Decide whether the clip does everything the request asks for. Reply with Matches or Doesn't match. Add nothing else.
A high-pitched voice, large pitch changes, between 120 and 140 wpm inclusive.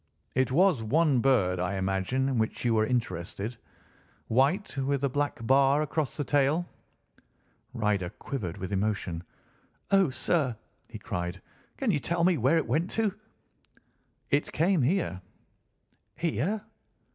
Doesn't match